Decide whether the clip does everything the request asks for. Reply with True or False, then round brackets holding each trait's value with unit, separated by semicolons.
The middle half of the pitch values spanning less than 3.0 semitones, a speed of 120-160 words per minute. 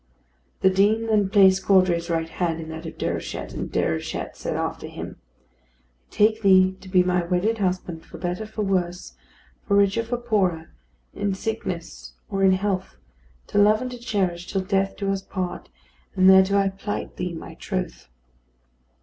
False (2.5 semitones; 170 wpm)